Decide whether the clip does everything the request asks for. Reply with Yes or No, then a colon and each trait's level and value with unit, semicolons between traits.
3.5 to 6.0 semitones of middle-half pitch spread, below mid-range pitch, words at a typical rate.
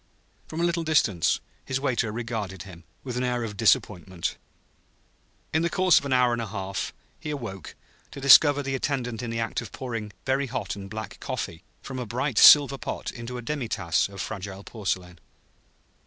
Yes: average, 5.2 semitones; low, 120 Hz; average, 185 wpm